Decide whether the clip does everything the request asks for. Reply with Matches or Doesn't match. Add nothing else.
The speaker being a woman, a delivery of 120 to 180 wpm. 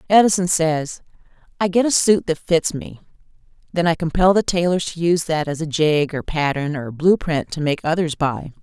Doesn't match